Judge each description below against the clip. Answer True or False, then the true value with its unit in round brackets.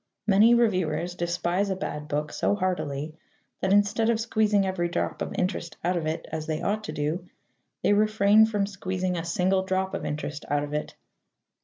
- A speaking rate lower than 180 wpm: False (185 wpm)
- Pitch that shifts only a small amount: False (4.0 semitones)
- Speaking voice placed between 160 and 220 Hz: True (185 Hz)